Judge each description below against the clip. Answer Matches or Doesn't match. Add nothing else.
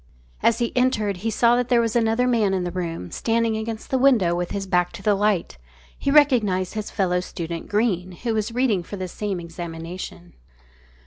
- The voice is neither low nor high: Doesn't match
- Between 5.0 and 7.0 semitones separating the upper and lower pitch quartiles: Doesn't match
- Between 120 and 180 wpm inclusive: Doesn't match